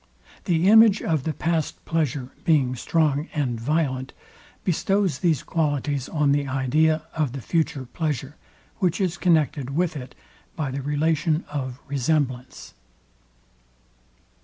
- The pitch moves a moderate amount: Yes, average, 3.4 semitones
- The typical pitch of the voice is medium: Yes, medium, 150 Hz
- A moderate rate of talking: No, slow, 125 wpm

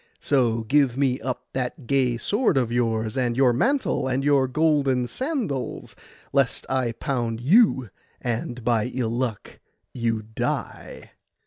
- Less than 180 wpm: Yes, slow, 135 wpm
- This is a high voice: No, low, 125 Hz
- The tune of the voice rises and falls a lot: No, average, 2.7 semitones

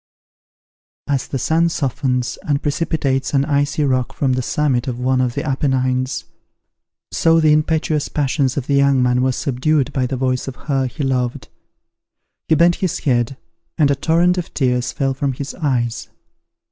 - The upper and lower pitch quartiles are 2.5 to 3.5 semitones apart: Yes, average, 2.8 semitones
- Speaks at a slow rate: No, average, 170 wpm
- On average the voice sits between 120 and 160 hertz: Yes, low, 135 Hz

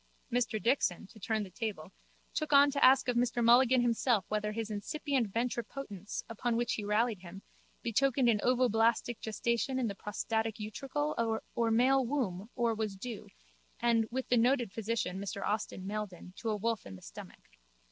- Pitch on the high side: Yes, high, 230 Hz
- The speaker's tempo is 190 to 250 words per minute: No, average, 170 wpm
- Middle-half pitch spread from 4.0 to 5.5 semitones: No, average, 2.9 semitones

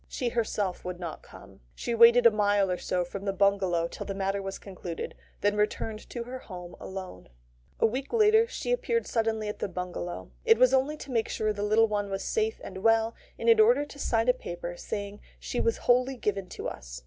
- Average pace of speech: No, fast, 215 wpm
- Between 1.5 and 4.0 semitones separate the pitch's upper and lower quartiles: No, average, 4.5 semitones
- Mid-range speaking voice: No, high, 210 Hz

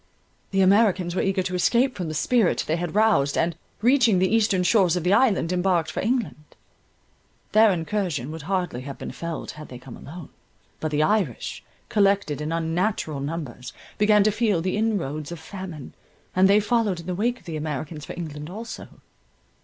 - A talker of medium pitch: Yes, medium, 180 Hz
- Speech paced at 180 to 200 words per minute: Yes, average, 185 wpm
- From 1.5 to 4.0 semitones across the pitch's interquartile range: No, average, 4.9 semitones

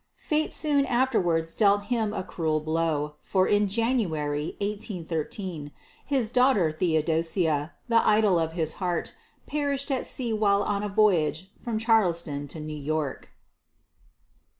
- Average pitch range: No, wide, 5.8 semitones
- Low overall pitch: No, high, 190 Hz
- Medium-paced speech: No, slow, 130 wpm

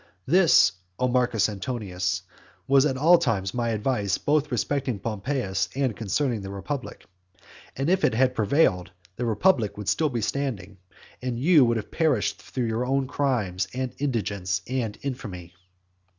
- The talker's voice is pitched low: Yes, low, 120 Hz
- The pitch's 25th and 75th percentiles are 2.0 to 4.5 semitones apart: No, average, 5.2 semitones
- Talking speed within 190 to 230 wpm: No, average, 150 wpm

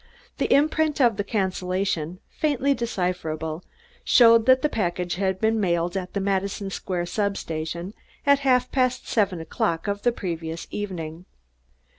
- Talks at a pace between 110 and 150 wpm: Yes, average, 140 wpm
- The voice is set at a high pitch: Yes, high, 195 Hz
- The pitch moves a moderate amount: Yes, average, 4.9 semitones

